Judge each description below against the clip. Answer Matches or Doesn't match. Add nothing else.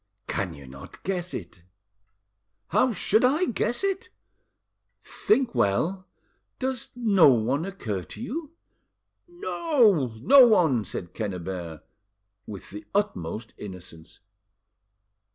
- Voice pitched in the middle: Matches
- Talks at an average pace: Doesn't match